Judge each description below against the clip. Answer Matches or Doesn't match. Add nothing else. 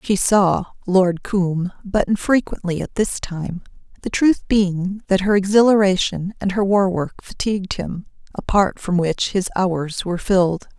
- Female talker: Matches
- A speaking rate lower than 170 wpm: Matches